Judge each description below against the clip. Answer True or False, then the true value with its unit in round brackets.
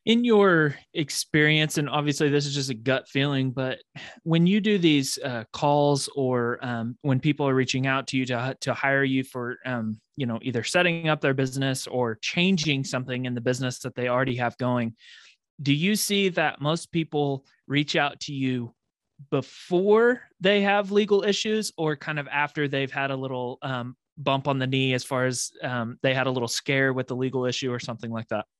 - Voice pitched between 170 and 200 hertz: False (135 Hz)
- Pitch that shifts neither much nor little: True (3.3 semitones)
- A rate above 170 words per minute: True (200 wpm)